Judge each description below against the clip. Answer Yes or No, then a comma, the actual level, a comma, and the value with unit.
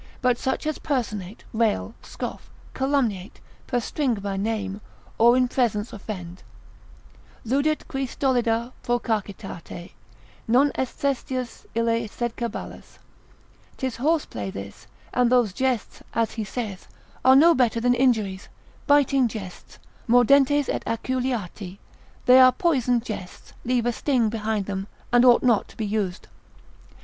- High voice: Yes, high, 235 Hz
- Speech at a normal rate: No, slow, 130 wpm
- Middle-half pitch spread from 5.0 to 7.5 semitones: No, average, 3.5 semitones